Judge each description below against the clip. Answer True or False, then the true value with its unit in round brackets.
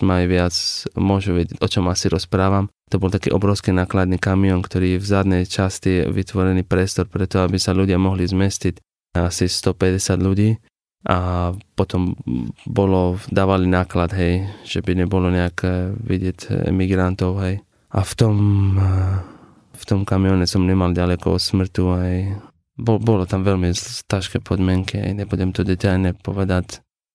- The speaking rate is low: False (145 wpm)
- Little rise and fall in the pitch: True (1.3 semitones)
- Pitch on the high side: False (95 Hz)